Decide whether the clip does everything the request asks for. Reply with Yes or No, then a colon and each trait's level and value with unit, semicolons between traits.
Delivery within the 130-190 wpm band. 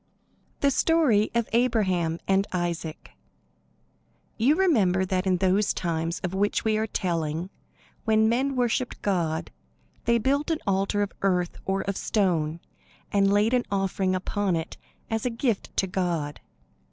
Yes: average, 145 wpm